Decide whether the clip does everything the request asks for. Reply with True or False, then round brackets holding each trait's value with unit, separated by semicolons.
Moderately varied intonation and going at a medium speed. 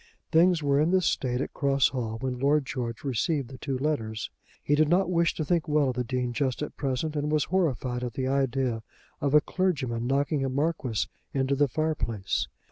False (3.4 semitones; 210 wpm)